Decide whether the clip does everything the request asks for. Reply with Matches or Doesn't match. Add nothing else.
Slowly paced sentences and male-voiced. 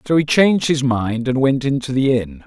Doesn't match